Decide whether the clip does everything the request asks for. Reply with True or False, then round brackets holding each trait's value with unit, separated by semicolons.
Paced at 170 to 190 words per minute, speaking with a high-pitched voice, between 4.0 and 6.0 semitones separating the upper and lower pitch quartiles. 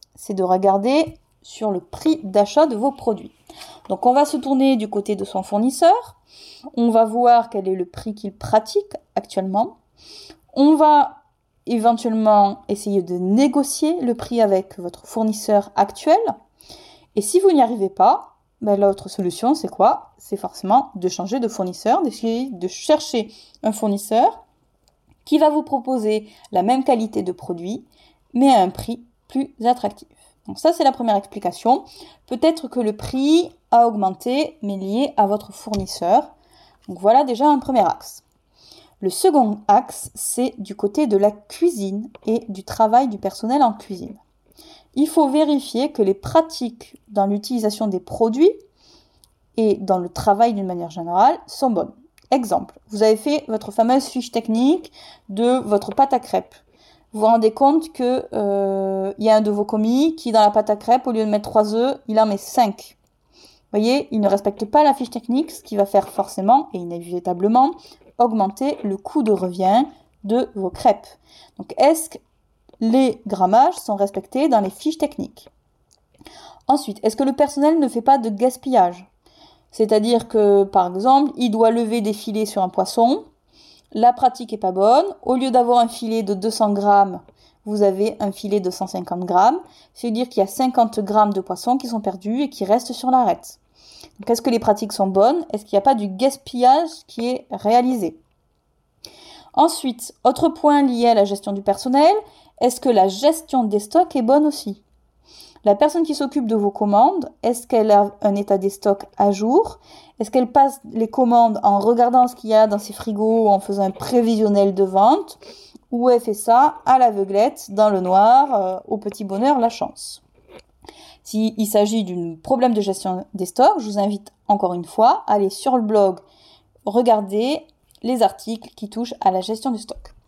True (180 wpm; 225 Hz; 4.8 semitones)